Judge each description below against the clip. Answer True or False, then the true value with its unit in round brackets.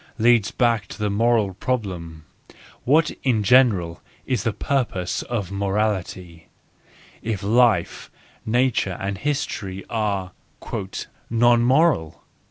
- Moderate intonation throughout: True (4.1 semitones)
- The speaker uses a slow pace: True (110 wpm)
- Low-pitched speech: True (105 Hz)